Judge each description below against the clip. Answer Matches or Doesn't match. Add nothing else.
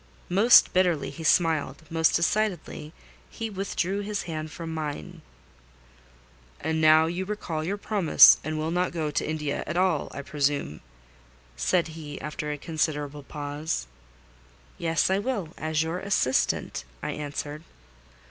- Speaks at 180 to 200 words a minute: Doesn't match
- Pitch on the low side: Doesn't match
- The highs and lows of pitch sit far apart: Doesn't match